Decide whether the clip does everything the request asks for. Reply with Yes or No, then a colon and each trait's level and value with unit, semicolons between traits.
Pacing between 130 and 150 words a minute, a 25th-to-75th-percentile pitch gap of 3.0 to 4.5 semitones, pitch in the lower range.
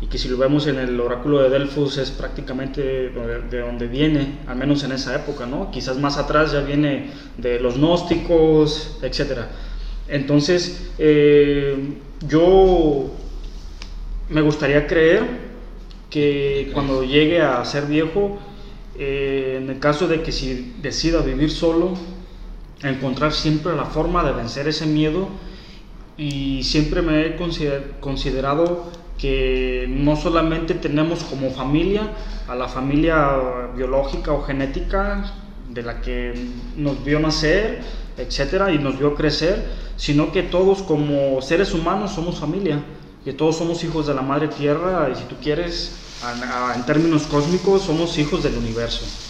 No: average, 140 wpm; average, 3.7 semitones; medium, 145 Hz